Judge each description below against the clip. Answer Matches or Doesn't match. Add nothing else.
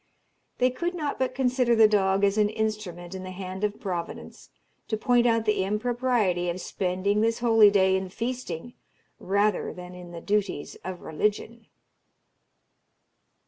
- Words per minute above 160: Doesn't match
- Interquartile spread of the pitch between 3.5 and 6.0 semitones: Matches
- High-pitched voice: Matches